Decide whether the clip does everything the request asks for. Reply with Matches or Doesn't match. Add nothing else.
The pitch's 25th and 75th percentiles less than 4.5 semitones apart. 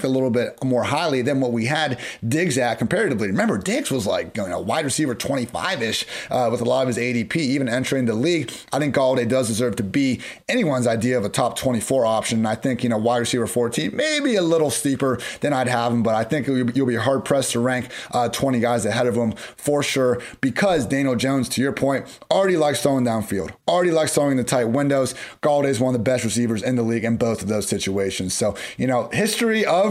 Matches